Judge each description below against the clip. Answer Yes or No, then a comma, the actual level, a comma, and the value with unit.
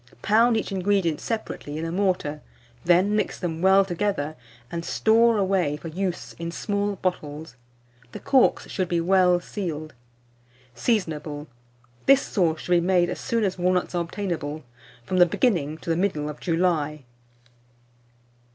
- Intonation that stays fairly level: No, average, 3.7 semitones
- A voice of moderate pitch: Yes, medium, 180 Hz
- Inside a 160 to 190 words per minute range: No, average, 150 wpm